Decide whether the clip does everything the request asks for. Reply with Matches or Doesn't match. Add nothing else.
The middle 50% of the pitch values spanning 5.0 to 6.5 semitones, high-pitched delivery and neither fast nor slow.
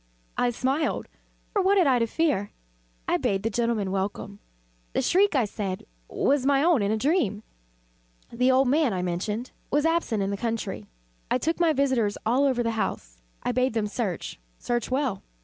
Matches